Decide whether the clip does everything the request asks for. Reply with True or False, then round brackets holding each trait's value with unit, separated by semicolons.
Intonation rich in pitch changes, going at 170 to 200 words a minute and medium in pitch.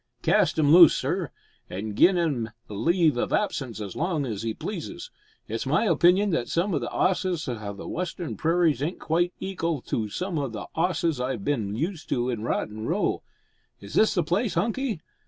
True (6.9 semitones; 180 wpm; 155 Hz)